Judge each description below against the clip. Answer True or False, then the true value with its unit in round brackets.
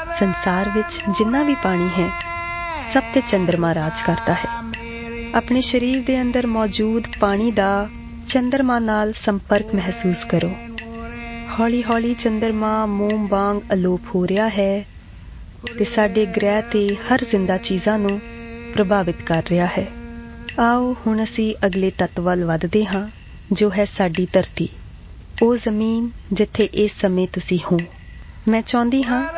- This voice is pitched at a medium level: False (215 Hz)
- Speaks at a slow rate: False (135 wpm)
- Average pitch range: True (3.6 semitones)